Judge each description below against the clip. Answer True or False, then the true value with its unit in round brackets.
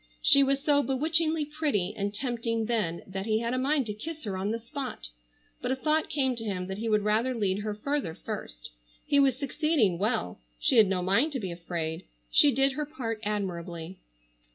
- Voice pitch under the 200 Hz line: False (225 Hz)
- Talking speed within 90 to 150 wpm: False (200 wpm)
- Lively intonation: True (6.3 semitones)